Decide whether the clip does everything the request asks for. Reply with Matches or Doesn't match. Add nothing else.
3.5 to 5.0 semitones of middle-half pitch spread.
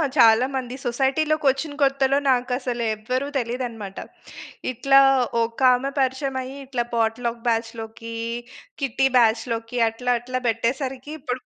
Doesn't match